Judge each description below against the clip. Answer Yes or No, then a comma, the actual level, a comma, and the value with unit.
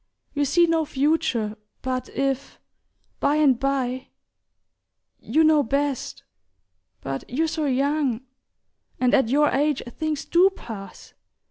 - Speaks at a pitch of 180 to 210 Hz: No, very high, 275 Hz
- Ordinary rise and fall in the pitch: Yes, average, 3.2 semitones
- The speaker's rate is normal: No, slow, 120 wpm